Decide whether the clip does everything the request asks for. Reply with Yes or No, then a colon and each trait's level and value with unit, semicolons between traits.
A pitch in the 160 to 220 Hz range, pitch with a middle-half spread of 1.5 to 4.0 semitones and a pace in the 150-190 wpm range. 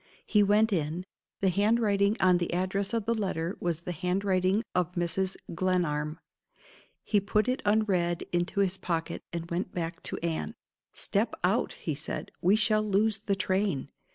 Yes: high, 190 Hz; average, 3.0 semitones; average, 160 wpm